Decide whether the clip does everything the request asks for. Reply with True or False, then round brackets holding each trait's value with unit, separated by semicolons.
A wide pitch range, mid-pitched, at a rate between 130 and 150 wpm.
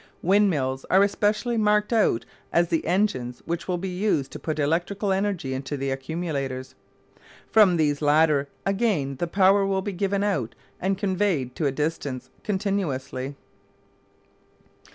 True (6.2 semitones; 170 Hz; 140 wpm)